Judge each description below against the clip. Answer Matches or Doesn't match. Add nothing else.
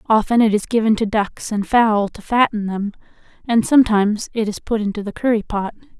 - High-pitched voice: Matches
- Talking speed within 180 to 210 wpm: Matches